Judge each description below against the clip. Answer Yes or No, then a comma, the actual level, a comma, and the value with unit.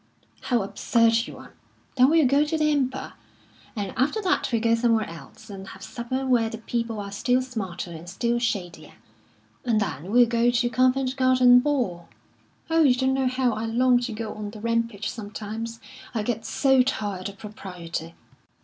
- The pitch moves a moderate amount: Yes, average, 3.5 semitones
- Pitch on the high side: Yes, high, 230 Hz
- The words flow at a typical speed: Yes, average, 180 wpm